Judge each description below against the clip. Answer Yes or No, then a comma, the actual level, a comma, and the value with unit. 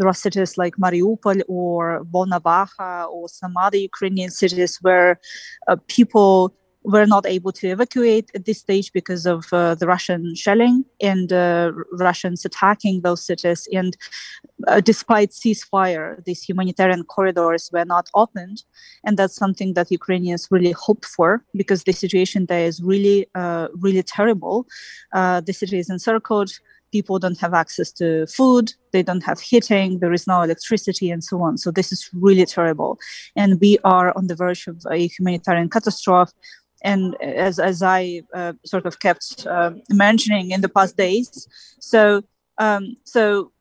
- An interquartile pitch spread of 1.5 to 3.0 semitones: Yes, narrow, 2.4 semitones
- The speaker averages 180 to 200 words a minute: No, average, 160 wpm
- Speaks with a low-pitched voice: No, medium, 185 Hz